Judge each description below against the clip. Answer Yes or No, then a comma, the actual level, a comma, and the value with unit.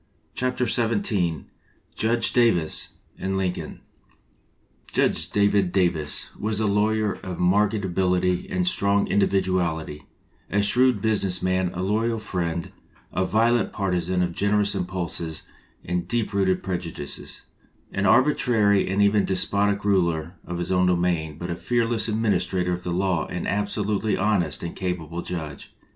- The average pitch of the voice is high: No, very low, 95 Hz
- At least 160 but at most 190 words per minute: No, slow, 135 wpm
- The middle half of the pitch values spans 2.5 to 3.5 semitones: Yes, average, 2.8 semitones